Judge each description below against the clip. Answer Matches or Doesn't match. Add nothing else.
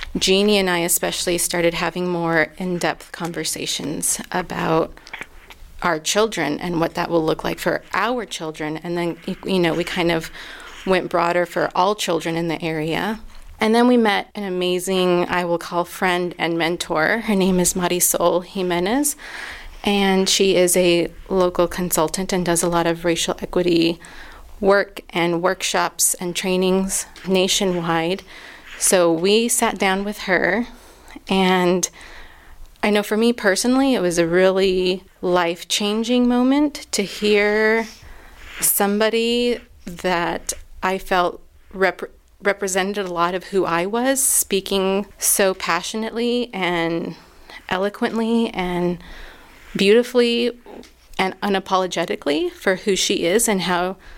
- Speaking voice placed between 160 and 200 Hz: Matches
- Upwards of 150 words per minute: Doesn't match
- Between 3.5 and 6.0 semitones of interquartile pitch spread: Doesn't match